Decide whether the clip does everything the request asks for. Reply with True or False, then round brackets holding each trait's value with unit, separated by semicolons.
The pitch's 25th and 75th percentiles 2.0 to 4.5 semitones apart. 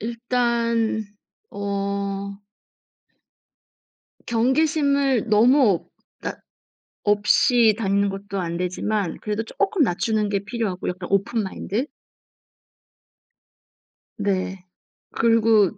True (2.9 semitones)